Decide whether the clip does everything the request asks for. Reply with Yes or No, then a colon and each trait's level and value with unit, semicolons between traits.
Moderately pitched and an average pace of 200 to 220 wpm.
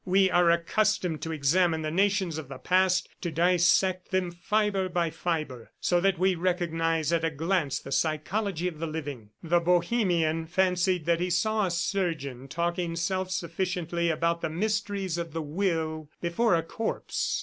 No: medium, 170 Hz; average, 165 wpm